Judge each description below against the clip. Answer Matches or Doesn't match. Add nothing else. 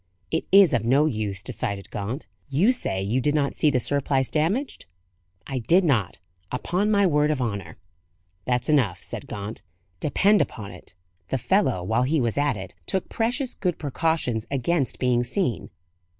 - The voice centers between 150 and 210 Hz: Doesn't match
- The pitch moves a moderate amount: Doesn't match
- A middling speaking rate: Matches